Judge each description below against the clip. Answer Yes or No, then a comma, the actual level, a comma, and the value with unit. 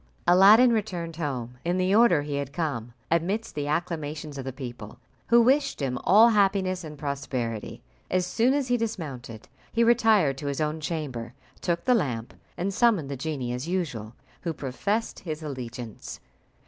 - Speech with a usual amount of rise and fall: No, wide, 6.7 semitones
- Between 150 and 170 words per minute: Yes, average, 165 wpm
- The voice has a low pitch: No, medium, 160 Hz